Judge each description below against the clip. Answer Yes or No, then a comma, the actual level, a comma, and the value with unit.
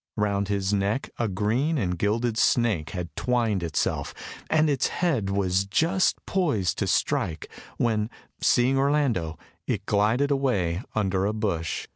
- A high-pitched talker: No, low, 105 Hz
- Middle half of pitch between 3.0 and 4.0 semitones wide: No, average, 4.9 semitones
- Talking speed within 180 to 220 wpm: No, average, 140 wpm